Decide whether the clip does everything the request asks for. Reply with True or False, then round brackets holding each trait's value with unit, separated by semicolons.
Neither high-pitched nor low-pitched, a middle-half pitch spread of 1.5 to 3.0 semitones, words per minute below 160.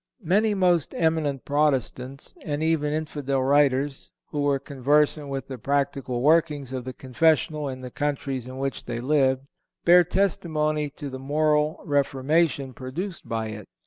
True (145 Hz; 2.6 semitones; 145 wpm)